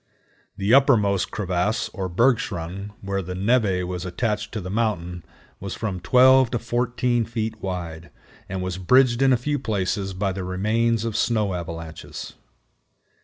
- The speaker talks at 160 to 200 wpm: No, average, 150 wpm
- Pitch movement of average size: Yes, average, 4.1 semitones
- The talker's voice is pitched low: Yes, low, 100 Hz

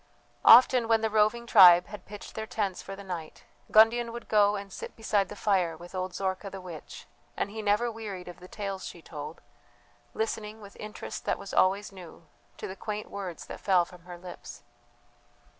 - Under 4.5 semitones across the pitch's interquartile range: Yes, average, 2.9 semitones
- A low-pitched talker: No, high, 200 Hz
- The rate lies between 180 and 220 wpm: Yes, average, 190 wpm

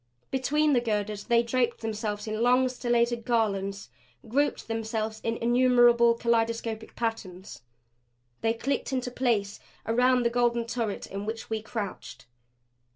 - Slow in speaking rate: Yes, slow, 130 wpm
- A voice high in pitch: Yes, high, 230 Hz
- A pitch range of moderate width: No, narrow, 1.9 semitones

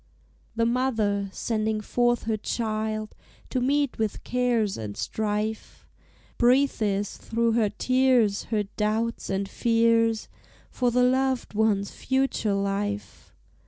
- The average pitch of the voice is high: Yes, high, 220 Hz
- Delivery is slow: Yes, slow, 115 wpm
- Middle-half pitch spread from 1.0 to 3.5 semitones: Yes, average, 2.8 semitones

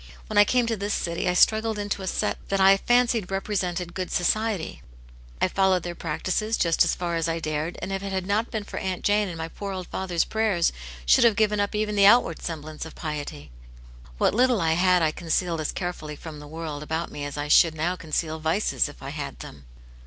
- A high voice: No, medium, 180 Hz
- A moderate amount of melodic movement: Yes, average, 4.2 semitones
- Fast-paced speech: Yes, fast, 225 wpm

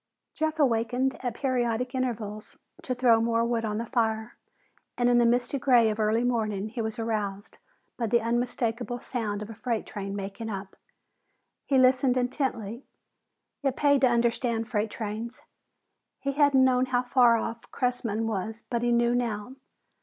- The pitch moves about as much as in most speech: No, narrow, 2.1 semitones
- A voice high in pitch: Yes, high, 235 Hz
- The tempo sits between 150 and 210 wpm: Yes, average, 160 wpm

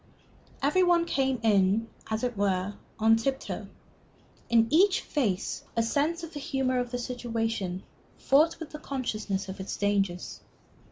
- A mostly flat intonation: No, wide, 5.6 semitones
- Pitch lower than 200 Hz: No, high, 235 Hz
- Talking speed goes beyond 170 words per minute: No, average, 150 wpm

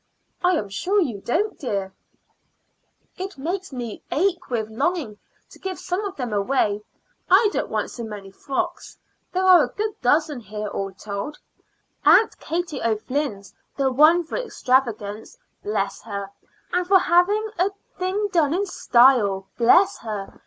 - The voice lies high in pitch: Yes, very high, 275 Hz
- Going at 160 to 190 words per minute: No, average, 150 wpm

